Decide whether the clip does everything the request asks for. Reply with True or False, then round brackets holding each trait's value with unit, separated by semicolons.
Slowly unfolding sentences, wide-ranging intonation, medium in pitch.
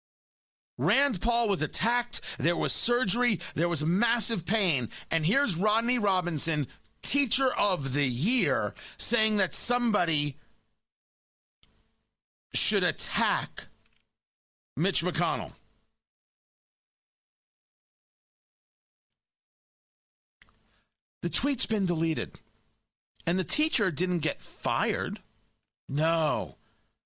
True (80 wpm; 7.1 semitones; 180 Hz)